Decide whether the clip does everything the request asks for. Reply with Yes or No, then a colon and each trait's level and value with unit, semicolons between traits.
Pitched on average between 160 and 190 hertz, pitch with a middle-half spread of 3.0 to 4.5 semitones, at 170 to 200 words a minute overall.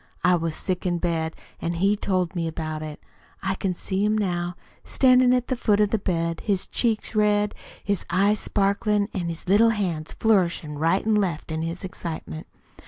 Yes: medium, 185 Hz; average, 3.8 semitones; average, 185 wpm